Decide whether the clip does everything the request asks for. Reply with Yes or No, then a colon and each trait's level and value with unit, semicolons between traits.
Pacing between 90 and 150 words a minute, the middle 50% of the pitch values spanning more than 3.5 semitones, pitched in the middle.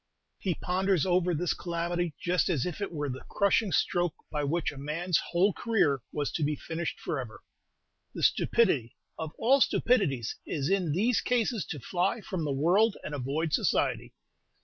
No: average, 170 wpm; average, 4.6 semitones; medium, 170 Hz